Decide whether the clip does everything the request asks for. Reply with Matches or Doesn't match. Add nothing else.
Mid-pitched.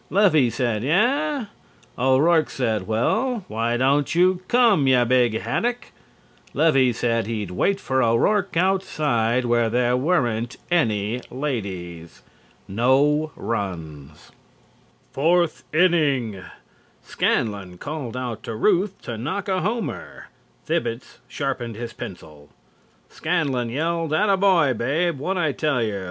Doesn't match